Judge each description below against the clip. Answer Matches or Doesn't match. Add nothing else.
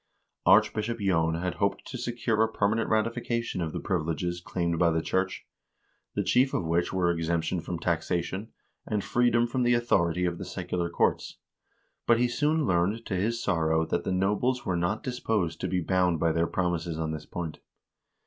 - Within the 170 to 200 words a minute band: Matches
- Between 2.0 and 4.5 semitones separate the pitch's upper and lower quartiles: Doesn't match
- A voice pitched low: Matches